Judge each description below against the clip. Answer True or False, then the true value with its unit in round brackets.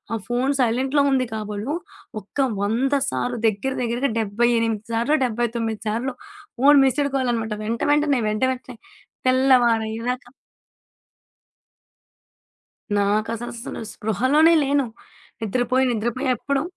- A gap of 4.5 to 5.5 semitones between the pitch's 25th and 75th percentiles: False (3.1 semitones)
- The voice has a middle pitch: False (240 Hz)